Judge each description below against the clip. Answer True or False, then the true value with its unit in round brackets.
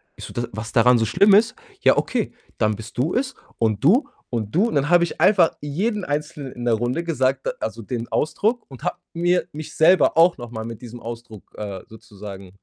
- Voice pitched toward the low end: True (130 Hz)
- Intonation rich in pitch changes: True (7.3 semitones)